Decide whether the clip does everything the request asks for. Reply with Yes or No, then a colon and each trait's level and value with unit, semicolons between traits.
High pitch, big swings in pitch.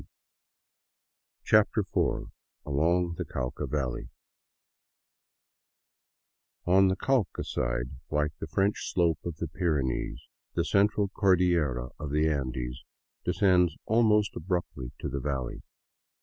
No: very low, 85 Hz; wide, 5.7 semitones